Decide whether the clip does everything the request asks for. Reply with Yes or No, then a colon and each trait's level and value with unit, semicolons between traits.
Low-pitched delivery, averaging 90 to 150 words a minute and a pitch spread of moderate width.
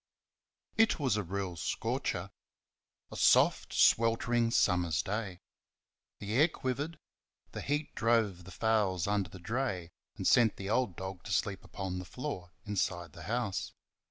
Yes: low, 100 Hz; average, 145 wpm; average, 4.5 semitones